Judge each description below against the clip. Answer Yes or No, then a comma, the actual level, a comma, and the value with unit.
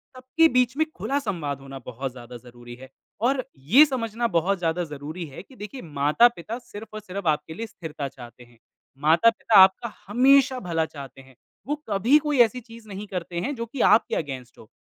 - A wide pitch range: Yes, wide, 8.9 semitones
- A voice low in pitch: No, high, 190 Hz